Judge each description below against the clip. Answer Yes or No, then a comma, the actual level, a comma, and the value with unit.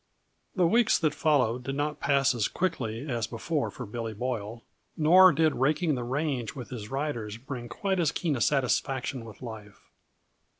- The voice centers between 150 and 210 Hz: No, low, 135 Hz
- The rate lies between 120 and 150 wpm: No, average, 175 wpm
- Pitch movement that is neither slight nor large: Yes, average, 4.7 semitones